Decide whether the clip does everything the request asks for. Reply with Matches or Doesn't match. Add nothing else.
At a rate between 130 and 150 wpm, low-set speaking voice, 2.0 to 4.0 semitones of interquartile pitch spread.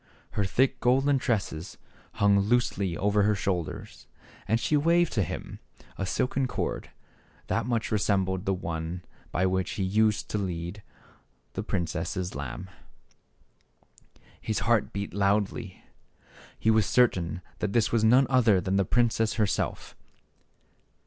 Matches